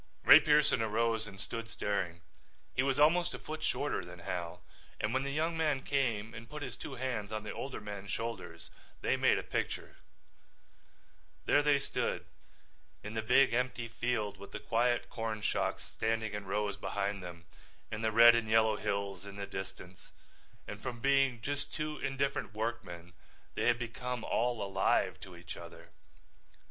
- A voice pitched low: Yes, low, 115 Hz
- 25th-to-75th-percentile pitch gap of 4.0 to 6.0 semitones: Yes, average, 4.3 semitones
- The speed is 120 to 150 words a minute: No, average, 170 wpm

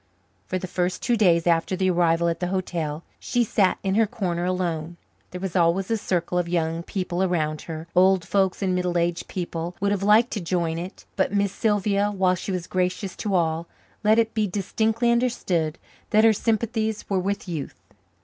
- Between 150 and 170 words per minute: No, average, 195 wpm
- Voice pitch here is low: No, medium, 185 Hz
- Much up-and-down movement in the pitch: No, average, 3.0 semitones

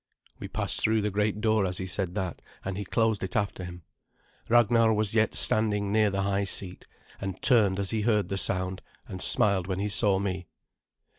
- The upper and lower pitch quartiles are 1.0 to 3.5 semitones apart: Yes, narrow, 2.4 semitones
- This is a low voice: Yes, low, 100 Hz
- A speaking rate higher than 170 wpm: Yes, average, 200 wpm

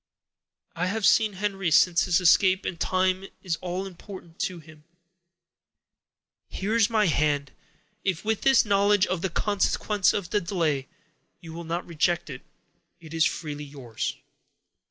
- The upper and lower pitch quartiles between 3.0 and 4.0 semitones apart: Yes, average, 3.3 semitones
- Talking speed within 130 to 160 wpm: Yes, average, 145 wpm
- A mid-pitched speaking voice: Yes, medium, 180 Hz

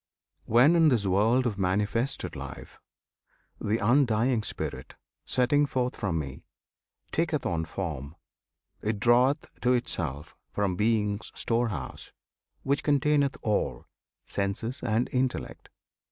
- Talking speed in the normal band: No, slow, 110 wpm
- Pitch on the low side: Yes, low, 115 Hz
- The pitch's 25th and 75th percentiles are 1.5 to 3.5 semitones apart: No, average, 4.6 semitones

